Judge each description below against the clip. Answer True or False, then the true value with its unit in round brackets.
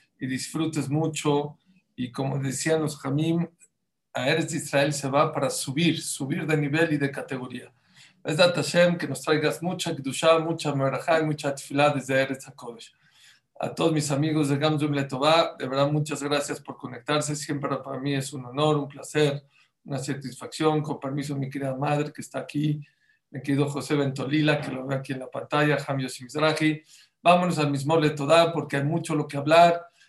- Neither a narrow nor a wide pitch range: False (2.1 semitones)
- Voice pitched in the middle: True (145 Hz)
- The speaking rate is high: False (180 wpm)